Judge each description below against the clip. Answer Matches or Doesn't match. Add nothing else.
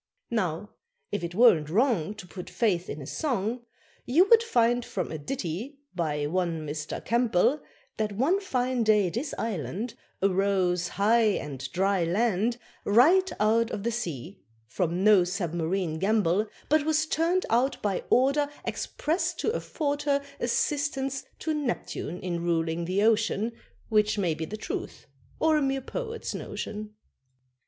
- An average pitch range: Doesn't match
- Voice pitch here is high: Matches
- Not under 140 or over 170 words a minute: Matches